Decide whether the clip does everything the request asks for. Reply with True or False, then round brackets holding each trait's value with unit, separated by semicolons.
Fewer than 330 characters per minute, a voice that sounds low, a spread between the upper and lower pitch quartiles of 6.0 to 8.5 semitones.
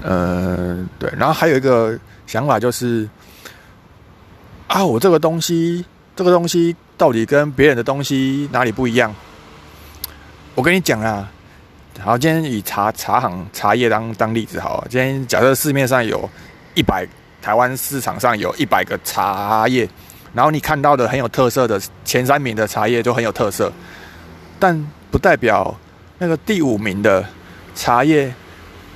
True (230 characters per minute; 120 Hz; 6.6 semitones)